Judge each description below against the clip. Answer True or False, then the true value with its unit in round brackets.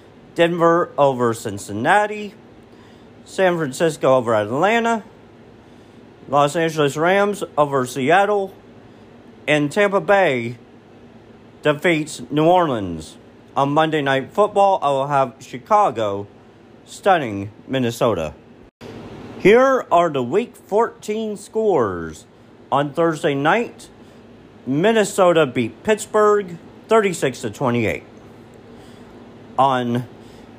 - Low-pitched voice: False (150 Hz)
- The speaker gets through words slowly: True (85 wpm)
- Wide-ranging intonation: True (8.3 semitones)